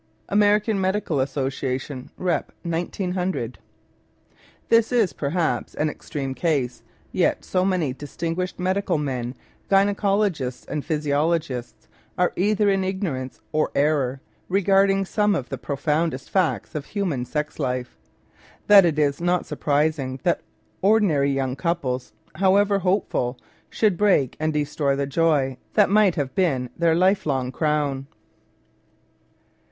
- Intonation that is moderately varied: No, wide, 5.7 semitones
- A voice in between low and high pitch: Yes, medium, 160 Hz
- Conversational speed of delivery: No, slow, 130 wpm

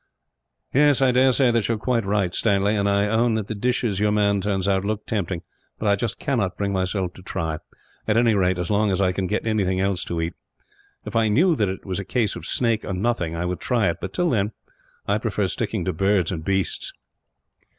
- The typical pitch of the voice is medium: No, low, 100 Hz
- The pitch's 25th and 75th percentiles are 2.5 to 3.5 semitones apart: Yes, average, 3.2 semitones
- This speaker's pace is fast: Yes, fast, 225 wpm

